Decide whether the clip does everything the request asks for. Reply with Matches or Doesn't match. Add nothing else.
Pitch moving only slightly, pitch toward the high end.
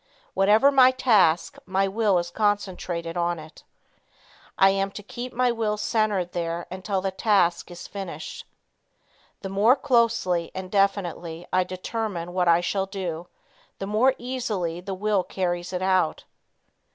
Doesn't match